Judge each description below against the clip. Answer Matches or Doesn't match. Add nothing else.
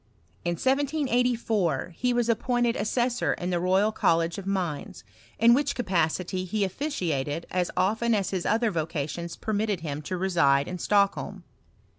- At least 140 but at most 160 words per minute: Matches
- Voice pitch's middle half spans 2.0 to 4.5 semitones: Doesn't match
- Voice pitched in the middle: Doesn't match